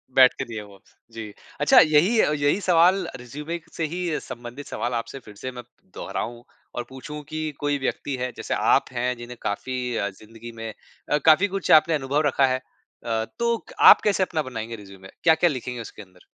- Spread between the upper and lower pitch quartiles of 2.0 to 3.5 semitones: No, average, 5.0 semitones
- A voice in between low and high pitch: No, low, 130 Hz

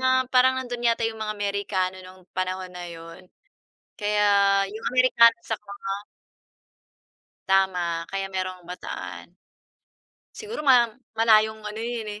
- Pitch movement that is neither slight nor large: Yes, average, 3.7 semitones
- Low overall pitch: No, high, 205 Hz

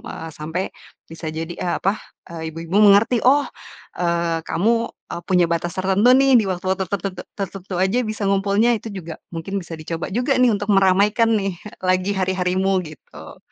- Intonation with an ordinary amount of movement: Yes, average, 3.2 semitones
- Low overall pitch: No, high, 190 Hz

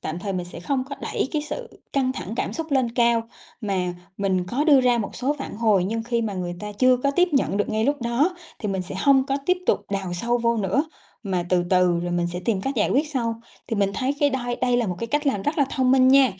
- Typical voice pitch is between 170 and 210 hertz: No, high, 235 Hz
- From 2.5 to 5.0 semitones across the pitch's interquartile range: No, wide, 5.5 semitones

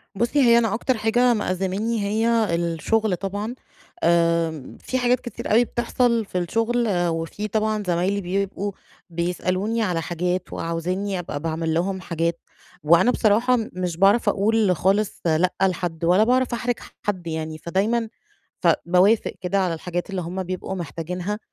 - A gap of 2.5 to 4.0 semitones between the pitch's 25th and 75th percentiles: No, average, 4.4 semitones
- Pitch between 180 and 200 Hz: Yes, high, 190 Hz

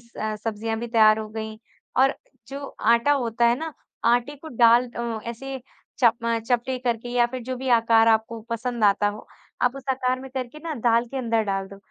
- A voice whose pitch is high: Yes, high, 235 Hz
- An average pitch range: No, narrow, 2.3 semitones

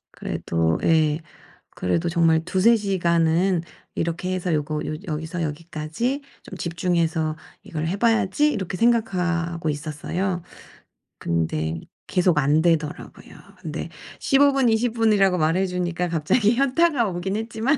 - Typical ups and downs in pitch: Yes, average, 4.5 semitones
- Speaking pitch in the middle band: Yes, medium, 175 Hz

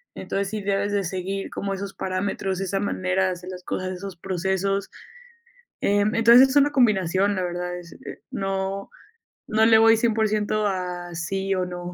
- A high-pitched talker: Yes, high, 195 Hz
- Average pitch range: No, narrow, 1.9 semitones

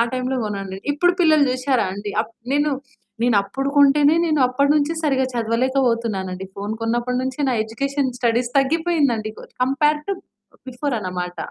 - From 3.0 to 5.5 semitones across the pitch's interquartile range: Yes, average, 3.9 semitones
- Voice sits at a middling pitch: No, very high, 255 Hz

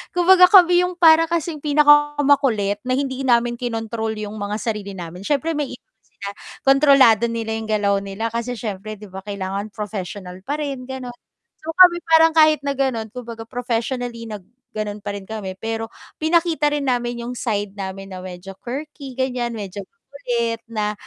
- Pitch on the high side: Yes, high, 235 Hz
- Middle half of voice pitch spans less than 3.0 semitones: No, average, 5.2 semitones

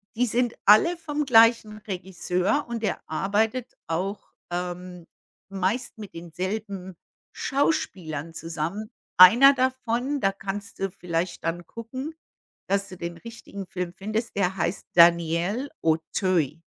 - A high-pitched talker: Yes, high, 195 Hz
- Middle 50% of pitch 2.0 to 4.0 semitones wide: No, average, 4.7 semitones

